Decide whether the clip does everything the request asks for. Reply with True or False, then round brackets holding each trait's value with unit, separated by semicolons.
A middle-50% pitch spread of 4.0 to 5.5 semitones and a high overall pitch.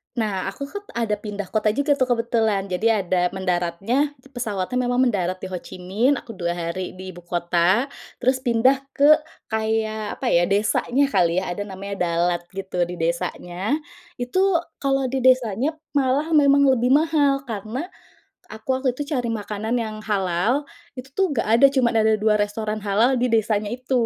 True (5.2 semitones; 220 Hz)